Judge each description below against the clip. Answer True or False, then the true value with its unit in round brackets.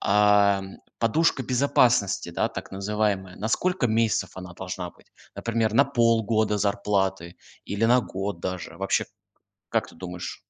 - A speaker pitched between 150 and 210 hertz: False (105 Hz)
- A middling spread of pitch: True (3.2 semitones)